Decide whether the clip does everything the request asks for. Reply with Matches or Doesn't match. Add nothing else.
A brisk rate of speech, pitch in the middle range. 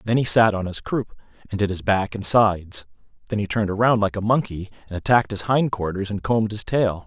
Doesn't match